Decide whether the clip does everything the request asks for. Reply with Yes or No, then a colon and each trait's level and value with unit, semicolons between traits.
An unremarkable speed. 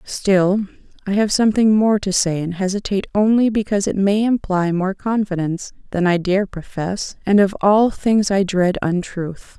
Yes: average, 170 wpm